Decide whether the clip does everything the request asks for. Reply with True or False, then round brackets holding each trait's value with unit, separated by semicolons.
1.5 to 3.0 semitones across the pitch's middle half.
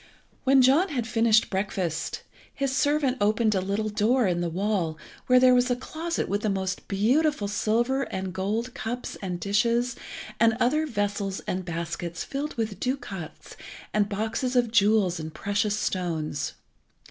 False (4.5 semitones)